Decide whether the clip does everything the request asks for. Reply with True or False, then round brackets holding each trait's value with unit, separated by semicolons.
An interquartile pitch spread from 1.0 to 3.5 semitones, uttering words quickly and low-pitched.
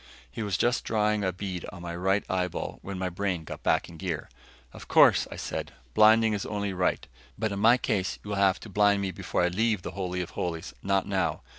True (2.5 semitones; 230 wpm; 100 Hz)